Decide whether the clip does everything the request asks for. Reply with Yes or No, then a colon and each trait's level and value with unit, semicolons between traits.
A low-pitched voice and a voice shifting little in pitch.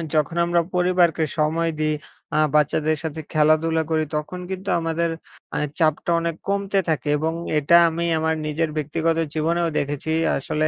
No: medium, 160 Hz; narrow, 1.6 semitones